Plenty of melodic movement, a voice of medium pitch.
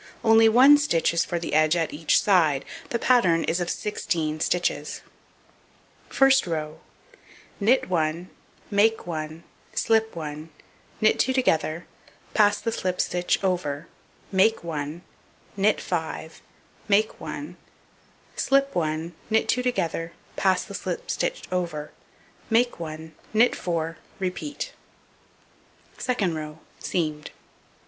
Yes: wide, 5.8 semitones; medium, 175 Hz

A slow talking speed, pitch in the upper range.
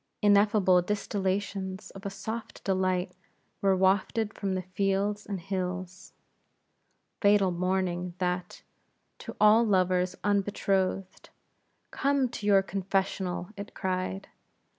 Yes: slow, 105 wpm; high, 195 Hz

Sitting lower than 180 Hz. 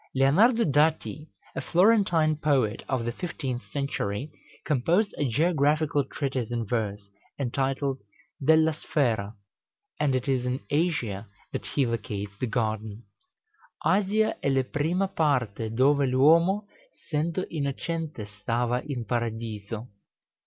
Yes: low, 135 Hz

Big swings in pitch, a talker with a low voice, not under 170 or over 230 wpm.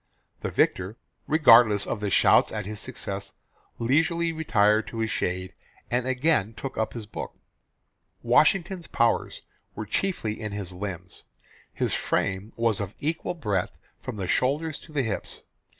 No: wide, 6.5 semitones; low, 115 Hz; average, 145 wpm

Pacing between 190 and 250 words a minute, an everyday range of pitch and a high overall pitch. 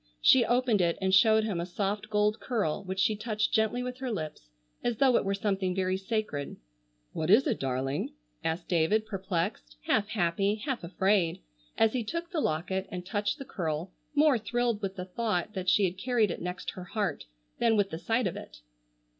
Yes: average, 195 wpm; average, 3.8 semitones; high, 200 Hz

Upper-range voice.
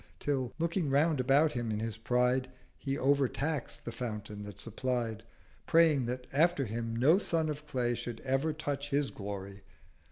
No: low, 130 Hz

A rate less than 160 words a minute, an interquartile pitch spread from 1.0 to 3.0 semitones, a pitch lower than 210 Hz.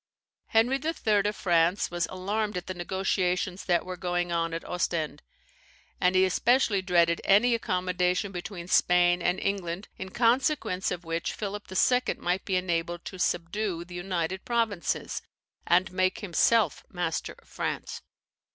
Yes: average, 145 wpm; narrow, 2.5 semitones; medium, 185 Hz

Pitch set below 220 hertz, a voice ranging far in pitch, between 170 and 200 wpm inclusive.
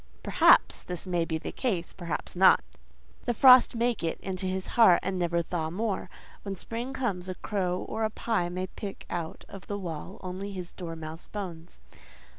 No: medium, 185 Hz; average, 3.1 semitones; average, 180 wpm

